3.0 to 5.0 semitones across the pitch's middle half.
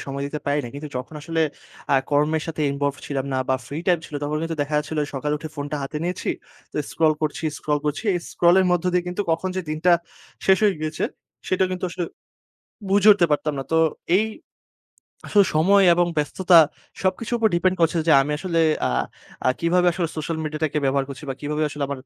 Yes: average, 3.3 semitones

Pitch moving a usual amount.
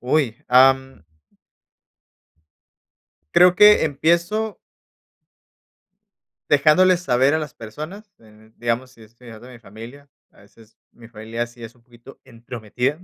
Yes: average, 4.9 semitones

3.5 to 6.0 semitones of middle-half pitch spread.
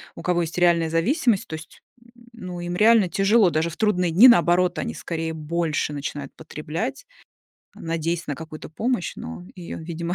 No: average, 2.9 semitones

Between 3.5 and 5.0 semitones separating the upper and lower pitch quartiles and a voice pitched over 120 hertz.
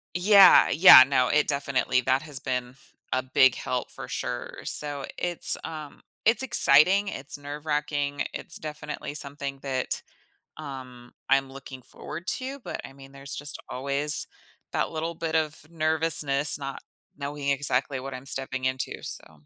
No: average, 2.7 semitones; medium, 140 Hz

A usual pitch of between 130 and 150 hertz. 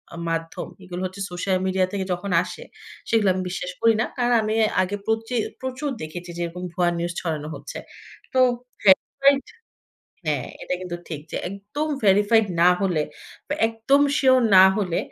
No: high, 190 Hz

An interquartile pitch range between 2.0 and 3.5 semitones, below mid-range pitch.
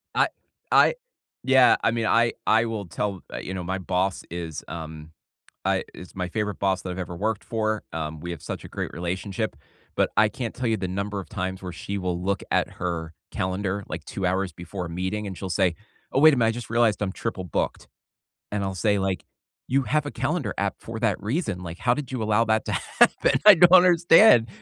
No: average, 3.9 semitones; low, 100 Hz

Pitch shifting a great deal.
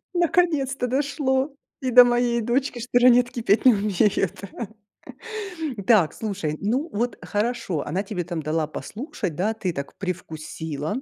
Yes: wide, 5.7 semitones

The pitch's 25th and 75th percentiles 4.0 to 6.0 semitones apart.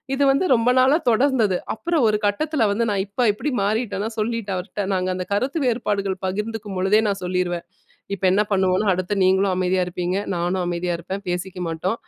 No: average, 3.6 semitones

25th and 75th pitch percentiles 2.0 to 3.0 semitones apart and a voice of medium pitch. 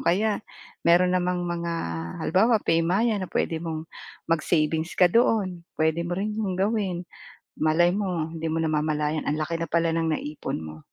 Yes: average, 2.7 semitones; medium, 170 Hz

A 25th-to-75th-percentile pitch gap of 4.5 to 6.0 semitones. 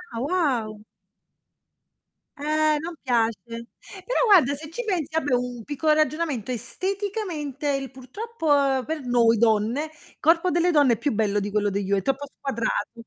Yes: wide, 5.5 semitones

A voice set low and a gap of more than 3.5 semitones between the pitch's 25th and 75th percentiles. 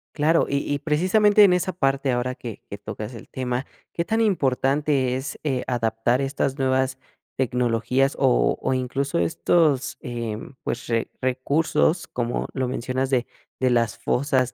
No: low, 130 Hz; average, 2.9 semitones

